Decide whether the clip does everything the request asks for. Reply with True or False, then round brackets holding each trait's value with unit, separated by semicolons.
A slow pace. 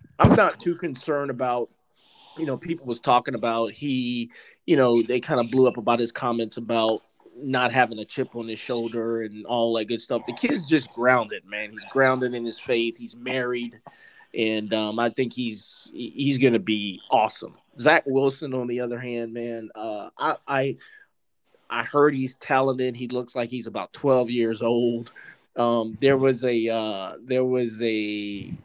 False (180 wpm)